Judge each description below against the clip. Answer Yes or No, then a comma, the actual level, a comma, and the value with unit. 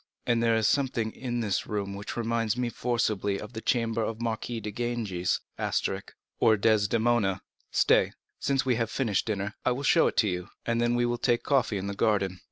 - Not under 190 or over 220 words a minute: Yes, average, 200 wpm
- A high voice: No, low, 115 Hz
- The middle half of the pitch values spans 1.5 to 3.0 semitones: Yes, average, 2.7 semitones